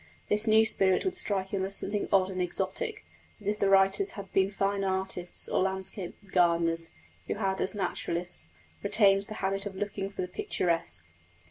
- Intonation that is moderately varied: No, narrow, 1.7 semitones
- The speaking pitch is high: Yes, high, 195 Hz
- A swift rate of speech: No, average, 175 wpm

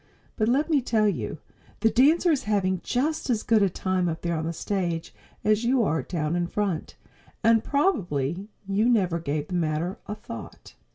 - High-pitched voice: Yes, high, 200 Hz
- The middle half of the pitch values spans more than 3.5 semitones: Yes, wide, 5.4 semitones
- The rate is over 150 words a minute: Yes, average, 185 wpm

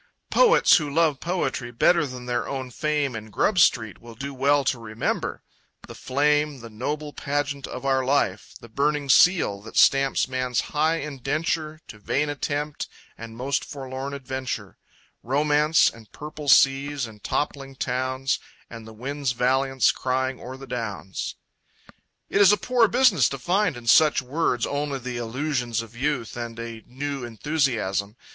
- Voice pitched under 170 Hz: Yes, low, 135 Hz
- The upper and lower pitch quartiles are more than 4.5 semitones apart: No, average, 3.5 semitones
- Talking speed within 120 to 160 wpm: Yes, average, 155 wpm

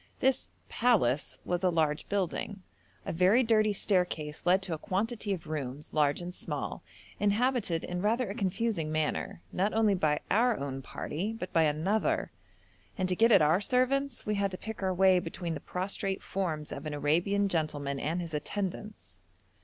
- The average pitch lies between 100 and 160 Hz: No, medium, 185 Hz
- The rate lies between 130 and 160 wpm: No, average, 175 wpm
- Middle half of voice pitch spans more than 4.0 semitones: Yes, average, 5.1 semitones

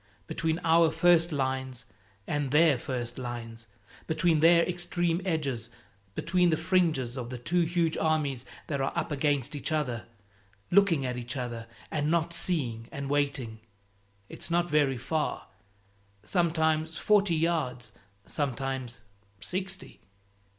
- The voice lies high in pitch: No, medium, 150 Hz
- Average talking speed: No, slow, 130 wpm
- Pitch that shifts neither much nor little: Yes, average, 4.7 semitones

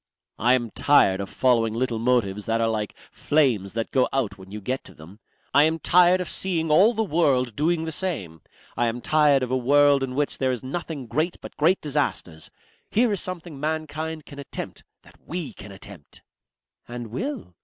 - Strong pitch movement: Yes, wide, 5.8 semitones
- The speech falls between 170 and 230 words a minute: Yes, average, 195 wpm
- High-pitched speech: No, low, 135 Hz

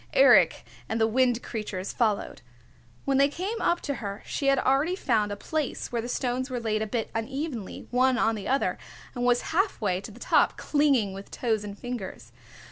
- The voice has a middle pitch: No, high, 245 Hz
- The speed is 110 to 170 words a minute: No, average, 200 wpm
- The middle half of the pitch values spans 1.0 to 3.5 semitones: No, average, 4.2 semitones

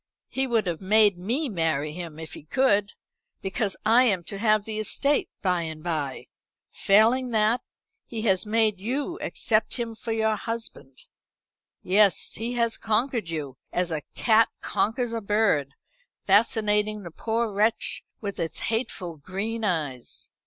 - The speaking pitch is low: No, high, 210 Hz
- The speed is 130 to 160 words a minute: Yes, average, 150 wpm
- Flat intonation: No, average, 4.3 semitones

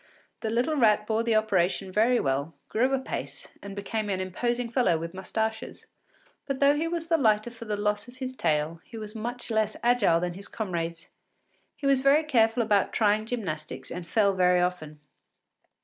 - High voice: Yes, high, 215 Hz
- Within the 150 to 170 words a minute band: No, average, 180 wpm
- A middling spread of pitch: Yes, average, 4.8 semitones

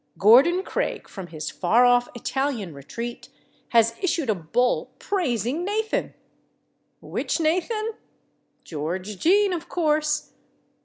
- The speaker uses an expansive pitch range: Yes, wide, 8.5 semitones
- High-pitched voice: Yes, very high, 250 Hz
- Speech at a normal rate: No, slow, 110 wpm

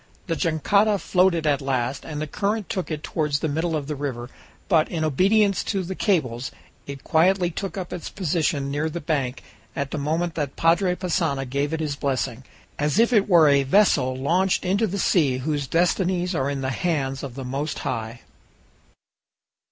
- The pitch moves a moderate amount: Yes, average, 4.5 semitones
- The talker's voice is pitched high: No, medium, 155 Hz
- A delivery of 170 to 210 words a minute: Yes, average, 185 wpm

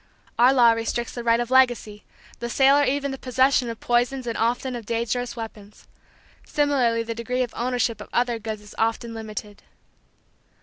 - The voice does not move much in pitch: Yes, narrow, 2.0 semitones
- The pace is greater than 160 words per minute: Yes, average, 175 wpm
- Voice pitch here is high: Yes, high, 235 Hz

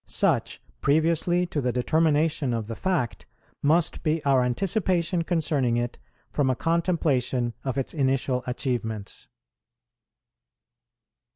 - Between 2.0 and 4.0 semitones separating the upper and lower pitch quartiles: No, average, 4.9 semitones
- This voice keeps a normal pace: No, slow, 110 wpm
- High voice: No, medium, 140 Hz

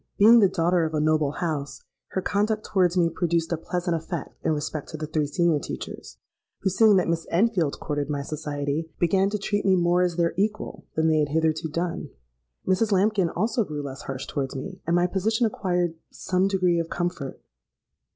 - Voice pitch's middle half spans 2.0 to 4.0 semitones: Yes, average, 3.5 semitones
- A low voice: No, medium, 170 Hz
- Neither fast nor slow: Yes, average, 195 wpm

